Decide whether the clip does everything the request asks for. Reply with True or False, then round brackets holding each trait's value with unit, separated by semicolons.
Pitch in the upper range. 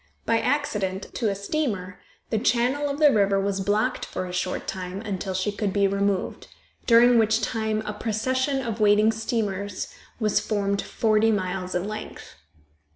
True (210 Hz)